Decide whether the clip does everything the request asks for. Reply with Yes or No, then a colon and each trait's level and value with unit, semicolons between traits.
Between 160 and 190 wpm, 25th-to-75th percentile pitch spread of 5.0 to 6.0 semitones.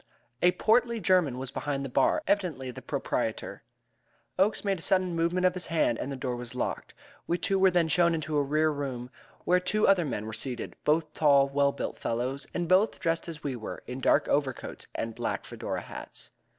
No: fast, 205 wpm; average, 5.3 semitones